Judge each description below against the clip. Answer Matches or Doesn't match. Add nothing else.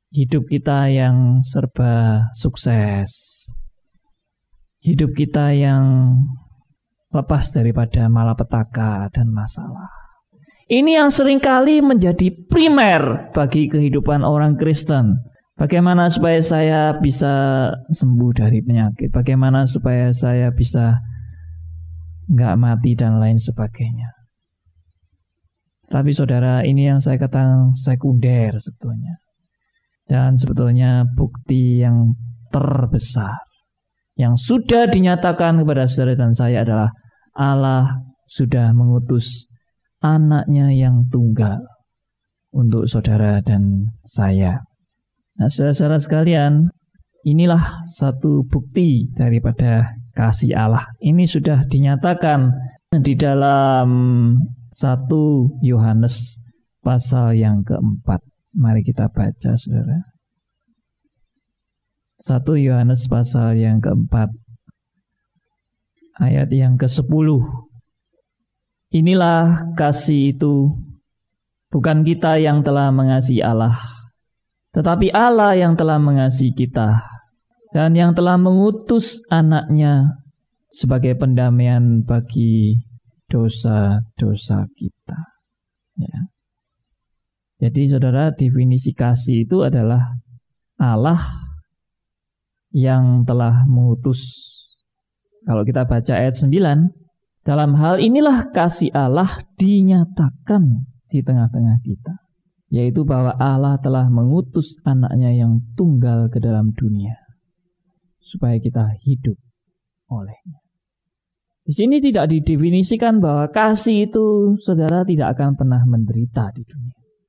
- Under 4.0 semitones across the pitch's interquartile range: Doesn't match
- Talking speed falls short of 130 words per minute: Matches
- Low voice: Matches